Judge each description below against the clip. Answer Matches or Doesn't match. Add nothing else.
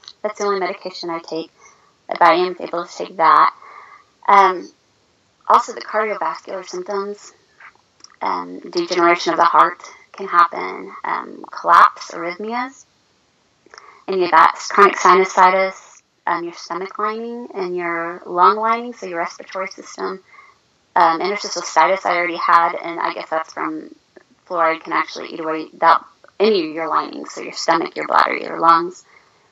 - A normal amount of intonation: Matches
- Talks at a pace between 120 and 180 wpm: Matches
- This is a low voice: Doesn't match